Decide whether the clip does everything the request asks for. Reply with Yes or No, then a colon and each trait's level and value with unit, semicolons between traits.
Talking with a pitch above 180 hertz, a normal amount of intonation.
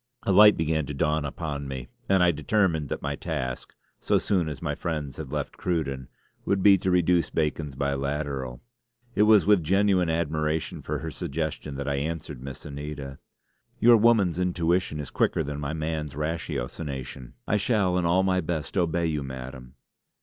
No: very low, 80 Hz; average, 4.0 semitones